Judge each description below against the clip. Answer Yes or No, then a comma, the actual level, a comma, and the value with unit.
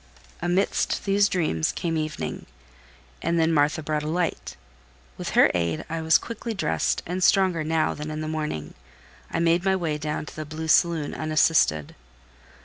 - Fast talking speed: No, average, 165 wpm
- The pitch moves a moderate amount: No, narrow, 2.2 semitones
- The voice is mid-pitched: Yes, medium, 160 Hz